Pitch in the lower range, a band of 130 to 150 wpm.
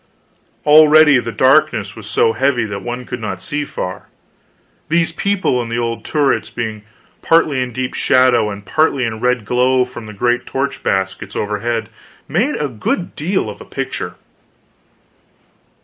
No: low, 125 Hz; average, 160 wpm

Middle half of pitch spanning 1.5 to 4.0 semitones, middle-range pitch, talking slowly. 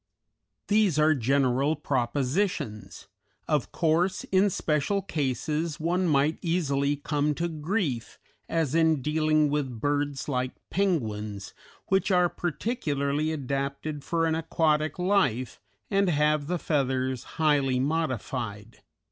Yes: average, 3.5 semitones; medium, 150 Hz; slow, 115 wpm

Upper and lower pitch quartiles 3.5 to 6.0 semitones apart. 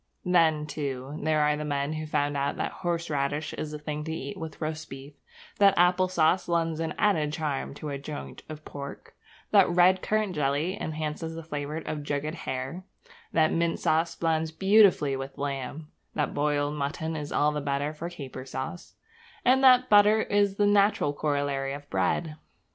No: average, 3.0 semitones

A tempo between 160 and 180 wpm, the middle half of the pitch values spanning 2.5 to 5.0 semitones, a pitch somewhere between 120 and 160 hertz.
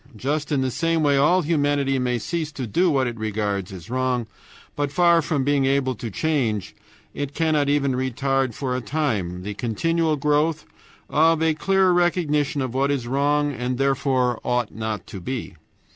Yes: average, 175 wpm; average, 3.6 semitones; medium, 140 Hz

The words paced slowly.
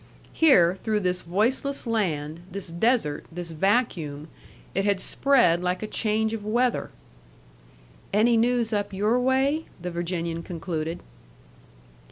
Yes: slow, 125 wpm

